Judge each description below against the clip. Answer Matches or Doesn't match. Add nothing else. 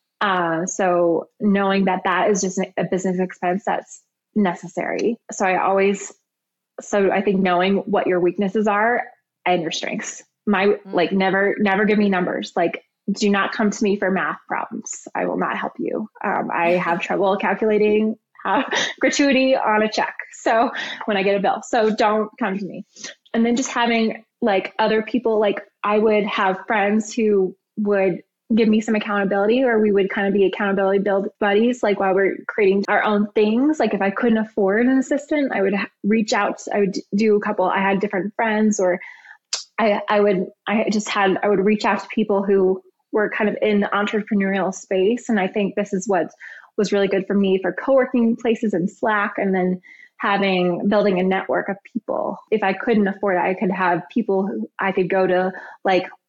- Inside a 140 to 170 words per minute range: Doesn't match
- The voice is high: Matches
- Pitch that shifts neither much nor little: Doesn't match